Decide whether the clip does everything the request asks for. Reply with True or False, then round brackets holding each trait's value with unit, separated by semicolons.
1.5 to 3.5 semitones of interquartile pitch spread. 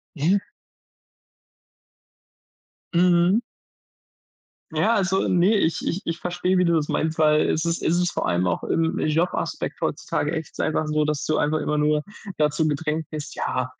True (2.6 semitones)